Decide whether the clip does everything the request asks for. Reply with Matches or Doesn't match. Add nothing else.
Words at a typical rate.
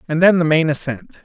Doesn't match